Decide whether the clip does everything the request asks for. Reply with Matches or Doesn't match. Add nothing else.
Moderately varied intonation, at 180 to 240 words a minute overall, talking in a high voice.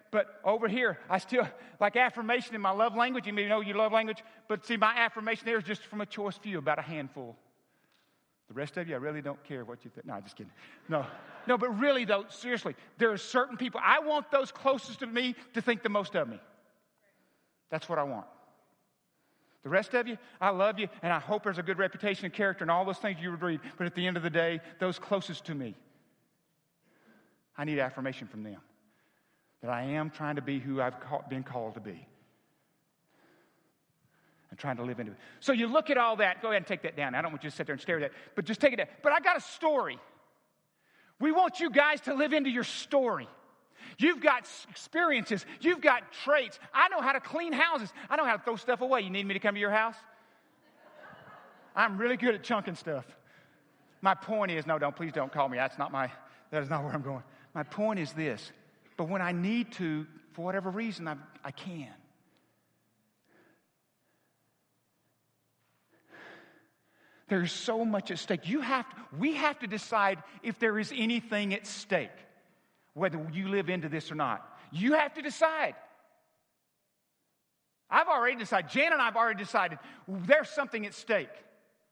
Doesn't match